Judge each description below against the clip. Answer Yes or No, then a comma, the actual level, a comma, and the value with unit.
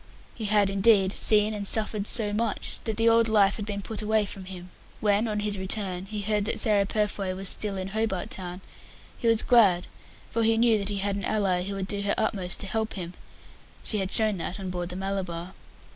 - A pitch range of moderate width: No, narrow, 2.2 semitones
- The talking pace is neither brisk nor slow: No, fast, 220 wpm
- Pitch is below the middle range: No, high, 205 Hz